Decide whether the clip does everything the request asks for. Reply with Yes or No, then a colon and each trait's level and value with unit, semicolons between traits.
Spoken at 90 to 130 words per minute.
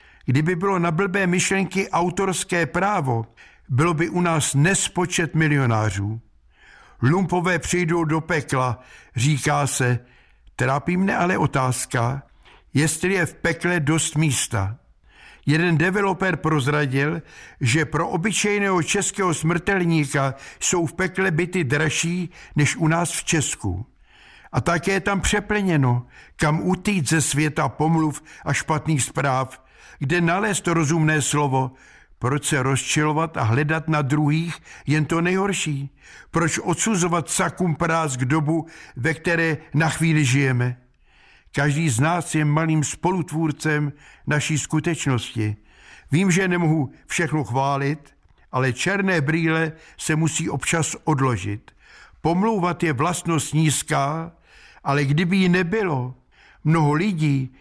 Yes: average, 120 wpm